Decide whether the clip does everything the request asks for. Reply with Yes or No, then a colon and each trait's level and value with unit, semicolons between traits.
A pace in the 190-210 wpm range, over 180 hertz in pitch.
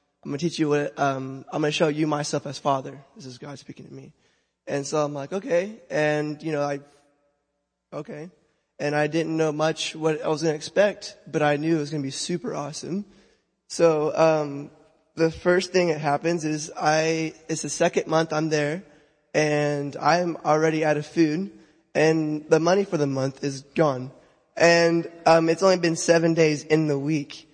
No: average, 200 wpm; medium, 155 Hz